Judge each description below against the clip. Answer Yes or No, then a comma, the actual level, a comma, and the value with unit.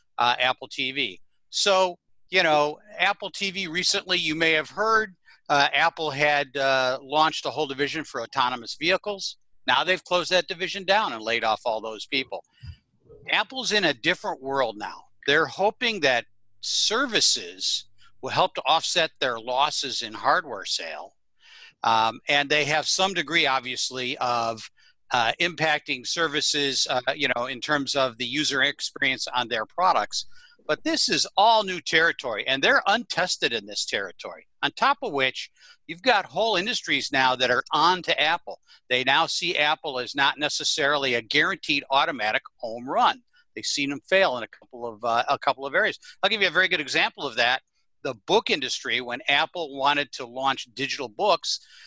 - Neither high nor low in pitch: Yes, medium, 145 Hz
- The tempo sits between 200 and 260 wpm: No, average, 175 wpm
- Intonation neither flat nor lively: No, wide, 5.7 semitones